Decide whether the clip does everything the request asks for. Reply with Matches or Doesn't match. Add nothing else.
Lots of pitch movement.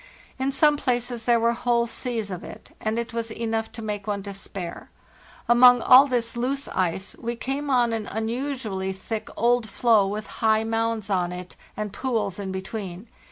Doesn't match